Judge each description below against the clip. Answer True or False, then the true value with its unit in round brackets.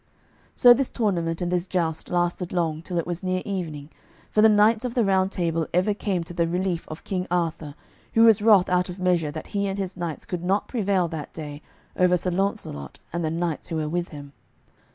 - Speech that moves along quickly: True (215 wpm)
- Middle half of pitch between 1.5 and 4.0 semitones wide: True (2.8 semitones)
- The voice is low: False (180 Hz)